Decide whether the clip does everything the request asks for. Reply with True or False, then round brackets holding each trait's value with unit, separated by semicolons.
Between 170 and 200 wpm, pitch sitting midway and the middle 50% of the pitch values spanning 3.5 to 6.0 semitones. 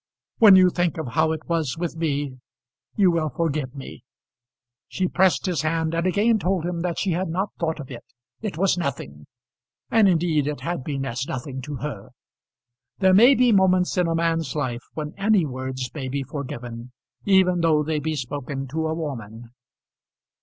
True (180 wpm; 160 Hz; 4.7 semitones)